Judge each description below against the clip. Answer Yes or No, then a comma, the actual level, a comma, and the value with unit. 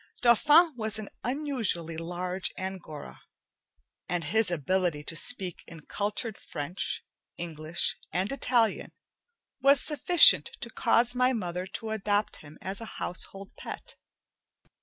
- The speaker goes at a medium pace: No, slow, 120 wpm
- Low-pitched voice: No, high, 195 Hz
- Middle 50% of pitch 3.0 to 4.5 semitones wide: No, wide, 5.6 semitones